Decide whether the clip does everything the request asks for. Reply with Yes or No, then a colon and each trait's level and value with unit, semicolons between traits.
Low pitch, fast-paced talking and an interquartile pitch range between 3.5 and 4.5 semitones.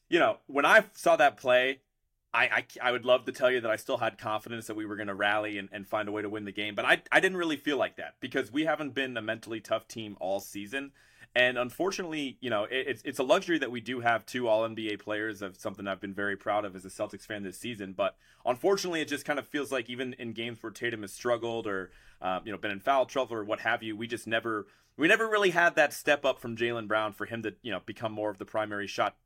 Yes: low, 115 Hz; fast, 275 wpm; average, 3.8 semitones